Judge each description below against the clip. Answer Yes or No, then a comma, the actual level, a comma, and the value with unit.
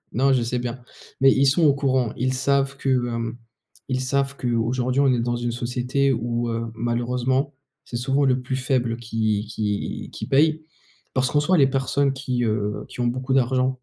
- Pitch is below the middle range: Yes, low, 125 Hz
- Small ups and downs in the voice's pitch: Yes, narrow, 2.3 semitones